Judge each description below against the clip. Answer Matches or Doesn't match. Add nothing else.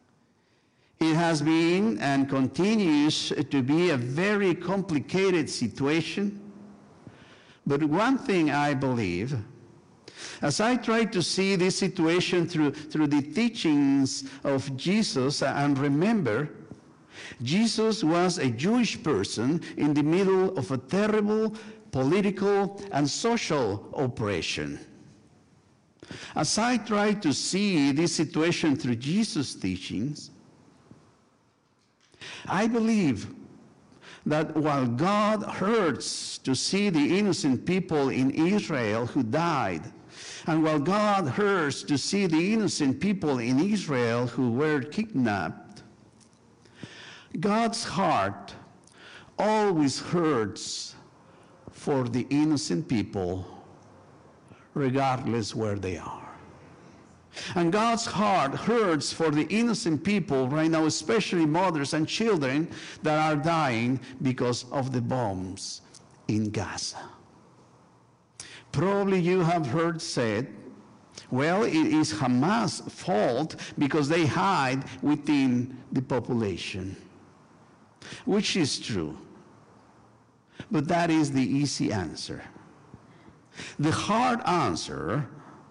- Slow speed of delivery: Matches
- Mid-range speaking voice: Matches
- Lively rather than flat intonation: Matches